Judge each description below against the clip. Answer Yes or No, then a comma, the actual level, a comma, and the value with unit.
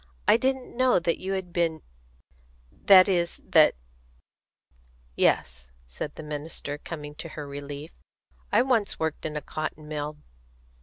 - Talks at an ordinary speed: Yes, average, 145 wpm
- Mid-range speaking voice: Yes, medium, 155 Hz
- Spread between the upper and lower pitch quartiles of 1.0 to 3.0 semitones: No, average, 4.1 semitones